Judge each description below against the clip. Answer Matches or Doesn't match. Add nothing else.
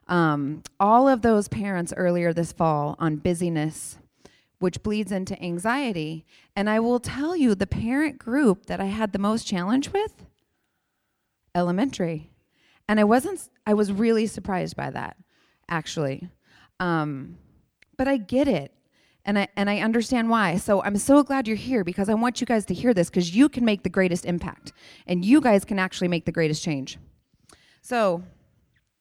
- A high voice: Matches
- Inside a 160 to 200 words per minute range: Matches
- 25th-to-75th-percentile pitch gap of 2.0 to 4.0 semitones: Doesn't match